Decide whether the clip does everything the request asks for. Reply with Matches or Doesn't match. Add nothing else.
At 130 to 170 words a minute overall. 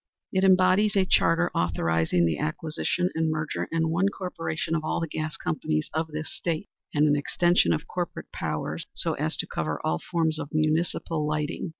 Doesn't match